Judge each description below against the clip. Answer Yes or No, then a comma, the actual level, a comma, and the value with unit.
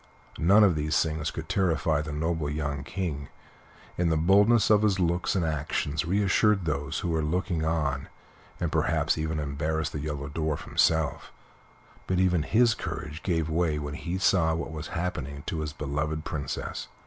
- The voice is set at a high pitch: No, very low, 80 Hz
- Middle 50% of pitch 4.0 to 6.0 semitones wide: No, average, 3.0 semitones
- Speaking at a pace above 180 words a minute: No, average, 170 wpm